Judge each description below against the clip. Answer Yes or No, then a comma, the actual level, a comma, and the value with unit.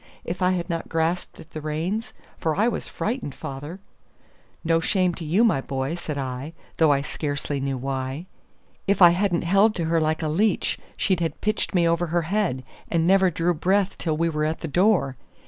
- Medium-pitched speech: Yes, medium, 165 Hz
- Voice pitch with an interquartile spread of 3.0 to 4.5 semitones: Yes, average, 3.4 semitones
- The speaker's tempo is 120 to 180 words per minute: No, fast, 205 wpm